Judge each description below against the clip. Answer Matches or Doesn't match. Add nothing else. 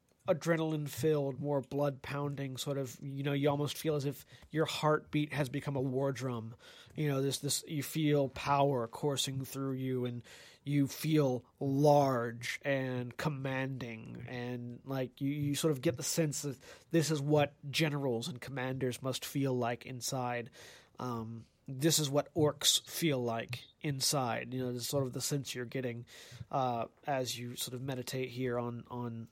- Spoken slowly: Doesn't match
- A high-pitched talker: Doesn't match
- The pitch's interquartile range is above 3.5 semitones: Doesn't match